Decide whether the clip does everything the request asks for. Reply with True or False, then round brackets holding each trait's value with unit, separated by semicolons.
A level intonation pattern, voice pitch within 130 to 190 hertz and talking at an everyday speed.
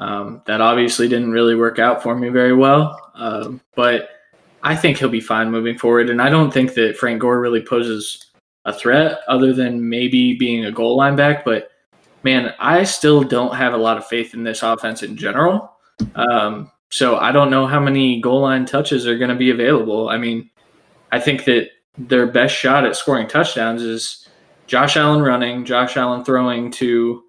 False (2.2 semitones; 120 Hz; 195 wpm)